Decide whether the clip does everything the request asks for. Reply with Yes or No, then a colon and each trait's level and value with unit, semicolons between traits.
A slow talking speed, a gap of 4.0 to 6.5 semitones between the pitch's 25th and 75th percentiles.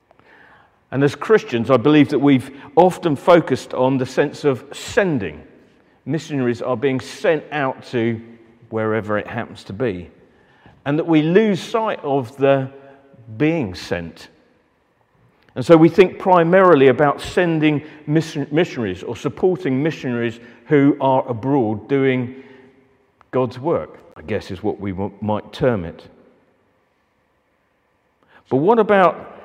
Yes: slow, 125 wpm; average, 4.7 semitones